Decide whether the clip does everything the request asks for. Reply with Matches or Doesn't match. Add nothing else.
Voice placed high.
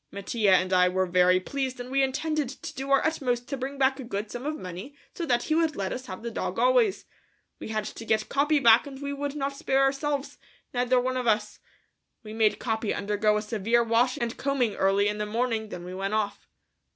Matches